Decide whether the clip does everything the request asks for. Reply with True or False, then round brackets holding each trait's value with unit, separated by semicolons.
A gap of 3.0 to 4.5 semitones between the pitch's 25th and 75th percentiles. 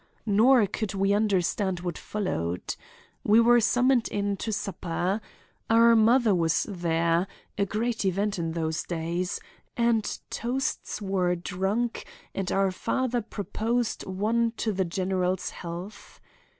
True (4.0 semitones)